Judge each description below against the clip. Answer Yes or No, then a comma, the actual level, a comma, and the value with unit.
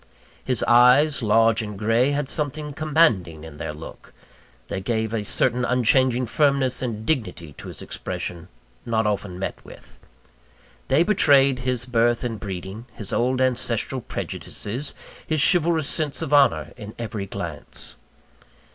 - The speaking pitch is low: Yes, low, 120 Hz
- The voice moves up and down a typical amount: Yes, average, 4.7 semitones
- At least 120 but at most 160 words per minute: Yes, average, 140 wpm